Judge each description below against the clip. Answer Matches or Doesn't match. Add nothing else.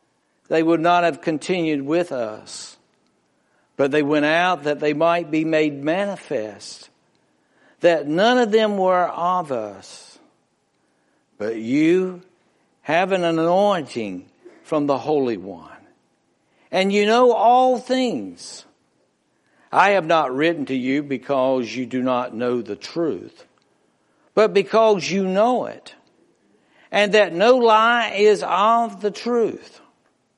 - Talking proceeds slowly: Matches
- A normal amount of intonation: Doesn't match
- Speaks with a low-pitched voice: Doesn't match